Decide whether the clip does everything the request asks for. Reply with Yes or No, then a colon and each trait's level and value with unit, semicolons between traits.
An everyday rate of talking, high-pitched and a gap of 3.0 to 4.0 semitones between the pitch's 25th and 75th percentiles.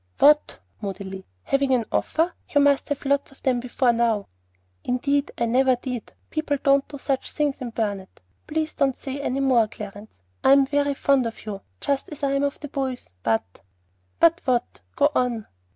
Yes: average, 185 wpm; very high, 265 Hz; average, 3.7 semitones